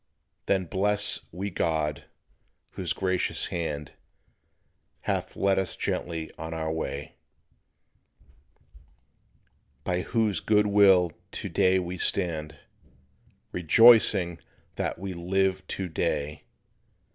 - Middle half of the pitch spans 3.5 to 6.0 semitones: No, average, 3.1 semitones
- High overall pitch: No, very low, 90 Hz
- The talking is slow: Yes, slow, 100 wpm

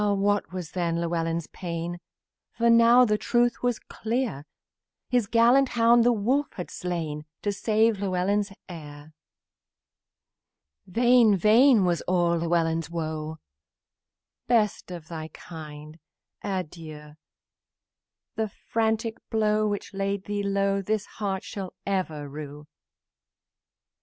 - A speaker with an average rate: No, slow, 110 wpm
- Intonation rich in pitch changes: No, average, 4.9 semitones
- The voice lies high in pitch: Yes, high, 195 Hz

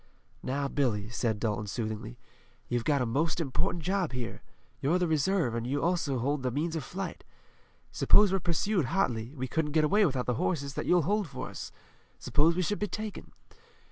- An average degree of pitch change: No, wide, 6.0 semitones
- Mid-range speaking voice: Yes, medium, 145 Hz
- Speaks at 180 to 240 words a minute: Yes, average, 190 wpm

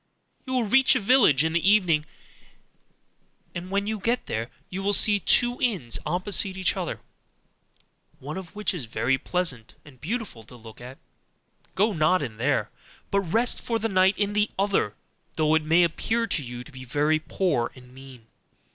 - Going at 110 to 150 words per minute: No, average, 180 wpm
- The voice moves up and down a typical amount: No, wide, 7.3 semitones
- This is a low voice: No, medium, 175 Hz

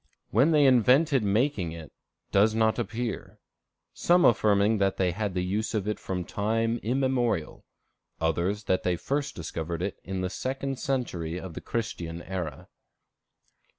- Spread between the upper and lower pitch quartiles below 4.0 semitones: No, average, 5.2 semitones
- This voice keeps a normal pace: Yes, average, 150 wpm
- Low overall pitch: Yes, low, 105 Hz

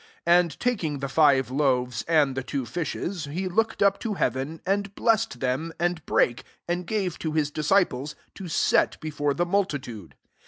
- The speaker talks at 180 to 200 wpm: Yes, average, 185 wpm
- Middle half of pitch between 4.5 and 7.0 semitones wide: Yes, average, 5.1 semitones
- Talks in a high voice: No, medium, 160 Hz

